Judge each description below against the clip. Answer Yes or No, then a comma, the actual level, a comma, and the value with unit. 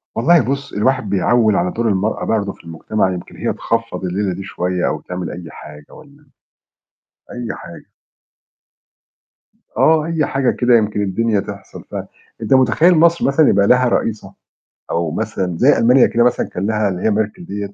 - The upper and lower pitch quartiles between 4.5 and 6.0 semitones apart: Yes, average, 4.9 semitones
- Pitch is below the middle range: Yes, low, 110 Hz